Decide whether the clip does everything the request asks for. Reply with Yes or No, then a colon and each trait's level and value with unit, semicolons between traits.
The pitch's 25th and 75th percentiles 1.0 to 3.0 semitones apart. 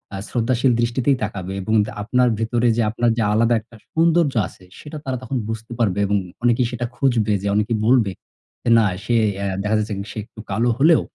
Yes: narrow, 2.6 semitones